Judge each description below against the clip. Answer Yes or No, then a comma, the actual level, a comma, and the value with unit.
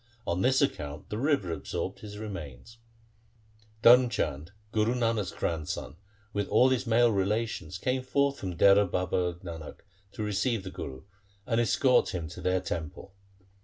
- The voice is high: No, low, 100 Hz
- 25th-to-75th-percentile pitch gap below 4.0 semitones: No, wide, 5.5 semitones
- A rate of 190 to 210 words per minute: No, average, 150 wpm